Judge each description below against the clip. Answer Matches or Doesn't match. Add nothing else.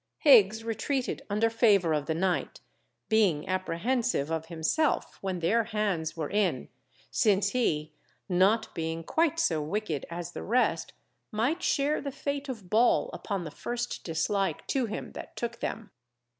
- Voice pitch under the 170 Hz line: Doesn't match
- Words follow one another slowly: Doesn't match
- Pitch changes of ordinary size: Doesn't match